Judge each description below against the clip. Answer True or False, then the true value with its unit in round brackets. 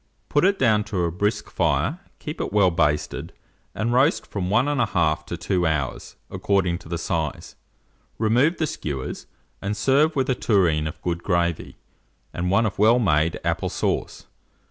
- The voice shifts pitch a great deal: True (5.9 semitones)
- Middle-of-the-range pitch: False (95 Hz)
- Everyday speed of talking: True (165 wpm)